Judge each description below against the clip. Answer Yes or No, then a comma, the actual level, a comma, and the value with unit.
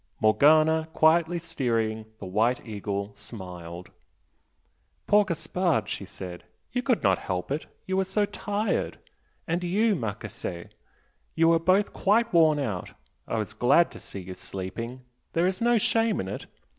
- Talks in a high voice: No, medium, 150 Hz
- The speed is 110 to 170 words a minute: Yes, average, 150 wpm